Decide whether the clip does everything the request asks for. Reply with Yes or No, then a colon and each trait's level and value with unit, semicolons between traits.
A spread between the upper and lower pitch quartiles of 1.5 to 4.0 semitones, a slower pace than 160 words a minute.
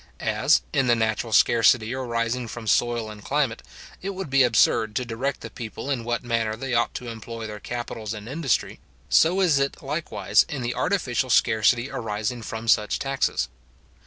No: average, 3.2 semitones; average, 175 wpm